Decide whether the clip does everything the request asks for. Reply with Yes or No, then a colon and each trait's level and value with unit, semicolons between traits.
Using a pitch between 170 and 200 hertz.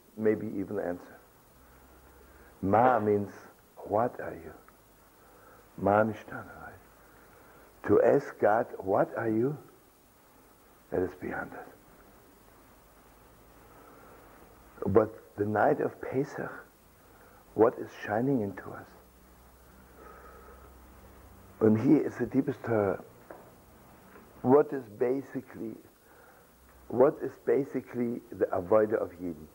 No: low, 100 Hz